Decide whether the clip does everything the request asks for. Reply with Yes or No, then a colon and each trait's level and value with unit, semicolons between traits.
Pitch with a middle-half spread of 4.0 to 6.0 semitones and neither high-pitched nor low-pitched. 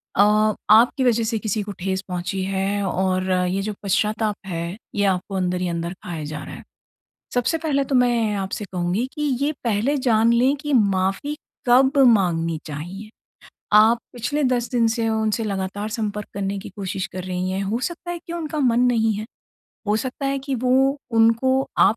No: average, 4.6 semitones; high, 215 Hz